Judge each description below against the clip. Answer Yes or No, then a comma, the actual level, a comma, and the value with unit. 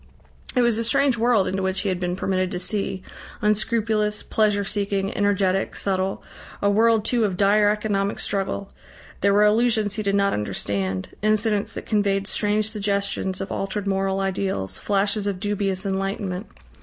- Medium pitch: No, high, 200 Hz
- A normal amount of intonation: No, narrow, 1.6 semitones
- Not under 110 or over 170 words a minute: Yes, average, 160 wpm